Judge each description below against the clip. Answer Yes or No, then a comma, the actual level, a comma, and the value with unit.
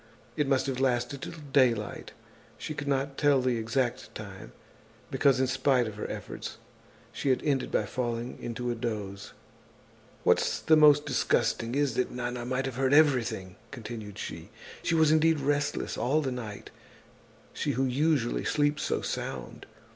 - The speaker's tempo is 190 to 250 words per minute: No, average, 155 wpm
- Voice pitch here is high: No, low, 130 Hz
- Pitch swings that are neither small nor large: Yes, average, 3.3 semitones